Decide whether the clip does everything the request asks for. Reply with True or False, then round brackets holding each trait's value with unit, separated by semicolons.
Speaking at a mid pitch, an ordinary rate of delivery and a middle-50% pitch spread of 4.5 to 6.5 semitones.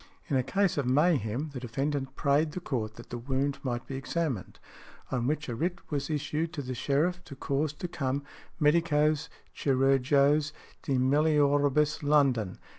False (145 Hz; 160 wpm; 2.5 semitones)